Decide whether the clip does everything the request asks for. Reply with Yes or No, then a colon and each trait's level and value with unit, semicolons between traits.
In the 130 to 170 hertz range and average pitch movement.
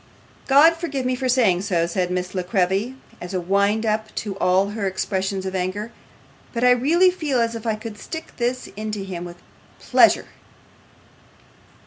No: high, 210 Hz; average, 4.8 semitones